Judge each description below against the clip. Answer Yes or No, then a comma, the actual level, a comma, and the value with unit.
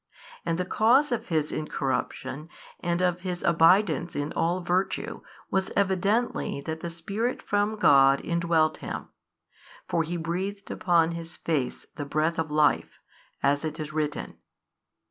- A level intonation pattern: No, average, 3.3 semitones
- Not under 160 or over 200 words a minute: No, average, 145 wpm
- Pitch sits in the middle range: Yes, medium, 170 Hz